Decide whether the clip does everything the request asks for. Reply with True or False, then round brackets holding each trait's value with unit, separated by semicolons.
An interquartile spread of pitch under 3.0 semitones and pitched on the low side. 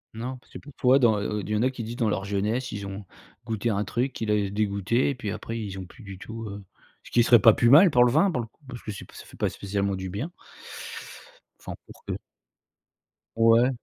False (3.4 semitones; 115 Hz)